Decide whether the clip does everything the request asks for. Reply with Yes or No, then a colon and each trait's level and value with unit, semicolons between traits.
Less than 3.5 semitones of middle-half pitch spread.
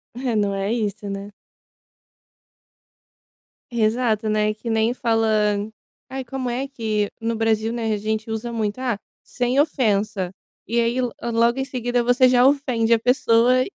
Yes: narrow, 2.4 semitones